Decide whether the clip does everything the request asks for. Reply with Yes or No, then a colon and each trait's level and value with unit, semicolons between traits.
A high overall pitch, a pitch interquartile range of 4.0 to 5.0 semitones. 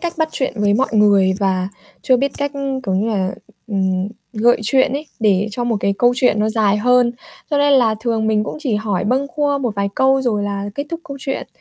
Yes: high, 225 Hz; average, 4.6 semitones